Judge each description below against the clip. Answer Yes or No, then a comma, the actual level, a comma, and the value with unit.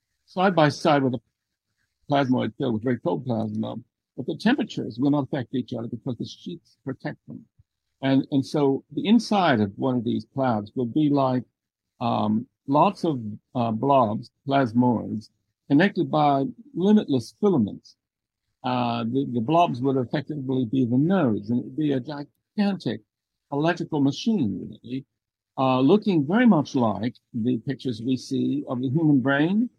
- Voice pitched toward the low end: Yes, low, 130 Hz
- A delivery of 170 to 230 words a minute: No, average, 155 wpm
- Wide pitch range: No, average, 4.0 semitones